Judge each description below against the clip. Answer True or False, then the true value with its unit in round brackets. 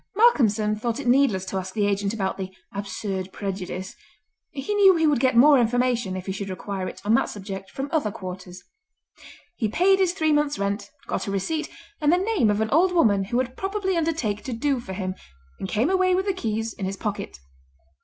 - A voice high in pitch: True (225 Hz)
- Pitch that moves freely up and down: True (7.5 semitones)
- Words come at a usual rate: False (210 wpm)